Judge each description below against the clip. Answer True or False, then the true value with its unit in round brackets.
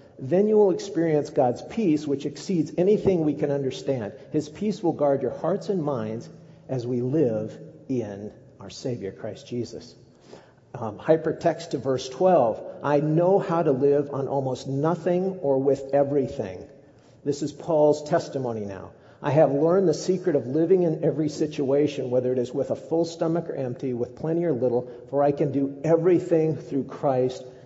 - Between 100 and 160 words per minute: False (170 wpm)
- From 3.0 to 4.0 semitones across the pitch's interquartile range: True (3.7 semitones)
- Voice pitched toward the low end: False (145 Hz)